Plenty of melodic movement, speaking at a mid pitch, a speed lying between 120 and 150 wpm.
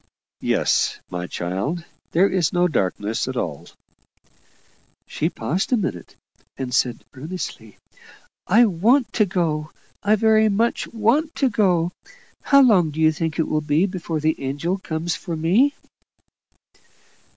Yes: wide, 5.7 semitones; medium, 170 Hz; average, 140 wpm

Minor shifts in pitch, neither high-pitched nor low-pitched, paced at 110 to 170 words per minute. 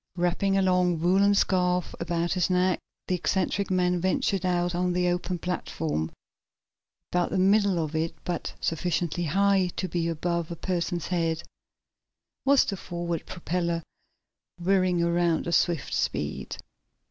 Yes: narrow, 1.4 semitones; medium, 175 Hz; average, 140 wpm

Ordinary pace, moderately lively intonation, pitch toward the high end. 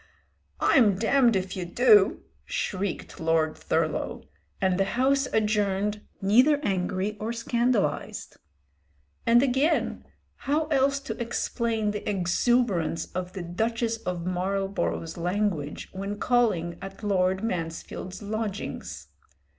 No: slow, 105 wpm; average, 4.3 semitones; high, 205 Hz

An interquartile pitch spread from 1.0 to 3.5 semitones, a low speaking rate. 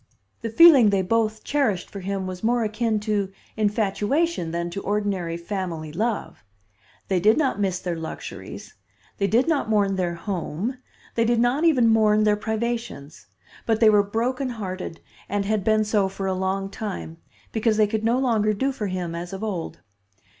No: average, 3.2 semitones; average, 175 wpm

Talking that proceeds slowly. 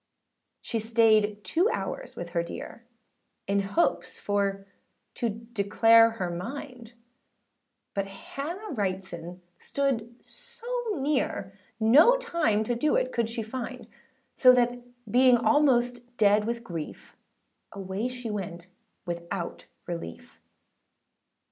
Yes: slow, 115 wpm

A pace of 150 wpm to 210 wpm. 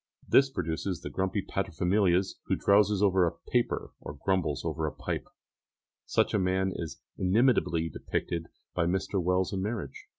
Yes: average, 155 wpm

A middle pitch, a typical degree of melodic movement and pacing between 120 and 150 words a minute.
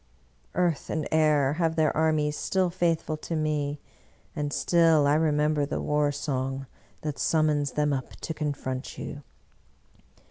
No: medium, 150 Hz; narrow, 1.7 semitones; average, 140 wpm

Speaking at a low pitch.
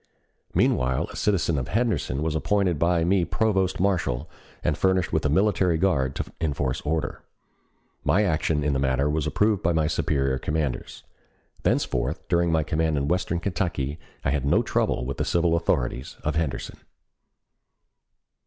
Yes: very low, 80 Hz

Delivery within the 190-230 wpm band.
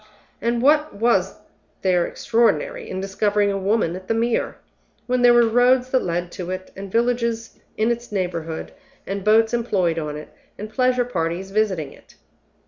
No: average, 165 wpm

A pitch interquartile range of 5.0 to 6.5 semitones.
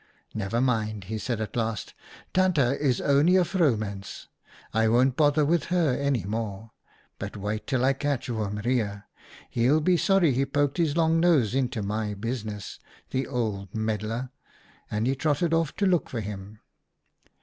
Yes: average, 5.3 semitones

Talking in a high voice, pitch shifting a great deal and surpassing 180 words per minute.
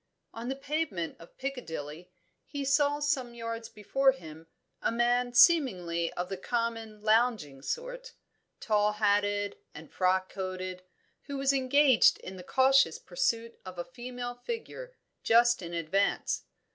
No: high, 230 Hz; wide, 6.3 semitones; slow, 135 wpm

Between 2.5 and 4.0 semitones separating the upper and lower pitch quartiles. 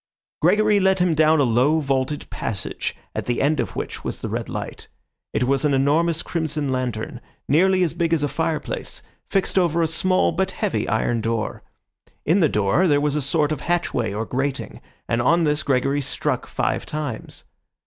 No: average, 4.6 semitones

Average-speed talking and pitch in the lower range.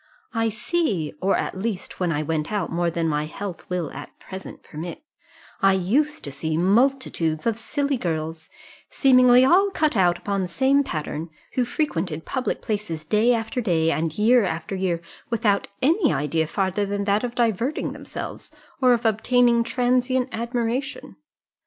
No: average, 160 wpm; high, 205 Hz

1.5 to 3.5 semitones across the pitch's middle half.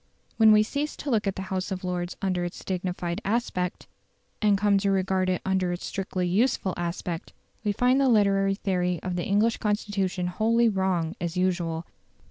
Yes: narrow, 2.5 semitones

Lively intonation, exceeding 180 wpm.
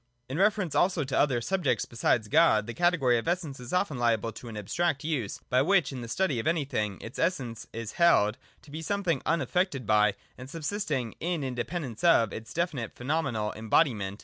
Yes: wide, 6.6 semitones; average, 195 wpm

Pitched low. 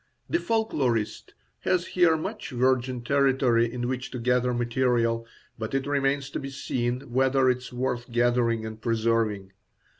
Yes: low, 125 Hz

